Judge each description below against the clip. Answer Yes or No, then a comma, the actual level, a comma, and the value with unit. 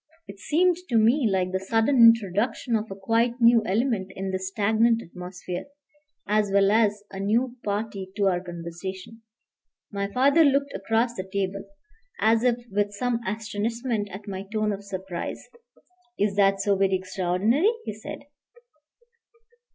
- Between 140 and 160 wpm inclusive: Yes, average, 150 wpm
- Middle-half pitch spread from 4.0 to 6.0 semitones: No, average, 3.2 semitones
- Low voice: No, high, 205 Hz